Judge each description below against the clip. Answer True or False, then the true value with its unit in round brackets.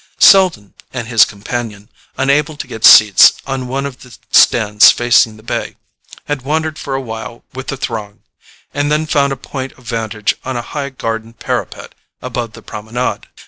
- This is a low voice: True (125 Hz)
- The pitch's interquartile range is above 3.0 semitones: True (3.6 semitones)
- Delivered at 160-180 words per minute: True (175 wpm)